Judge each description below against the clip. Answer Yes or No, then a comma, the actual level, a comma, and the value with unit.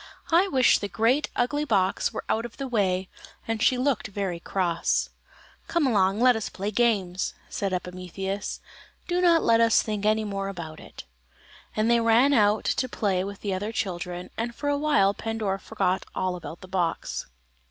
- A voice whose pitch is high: Yes, high, 210 Hz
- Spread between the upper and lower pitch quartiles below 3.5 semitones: No, average, 4.0 semitones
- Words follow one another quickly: No, average, 185 wpm